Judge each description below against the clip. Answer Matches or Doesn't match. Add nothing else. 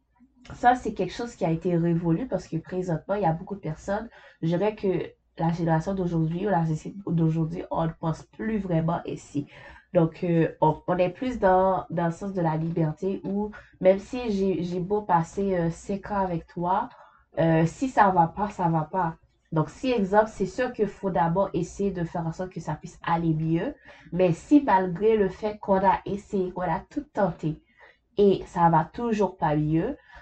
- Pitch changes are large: Doesn't match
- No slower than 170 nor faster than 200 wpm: Doesn't match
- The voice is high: Doesn't match